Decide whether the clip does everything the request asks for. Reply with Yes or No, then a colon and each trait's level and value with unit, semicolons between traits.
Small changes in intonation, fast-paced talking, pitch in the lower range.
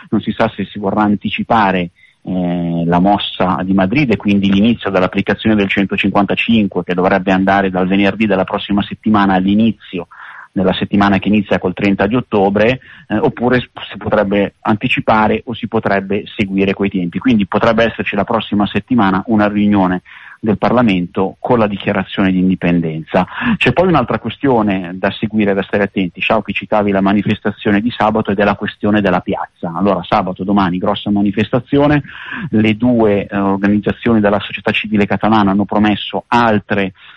No: narrow, 1.9 semitones; average, 160 wpm; low, 100 Hz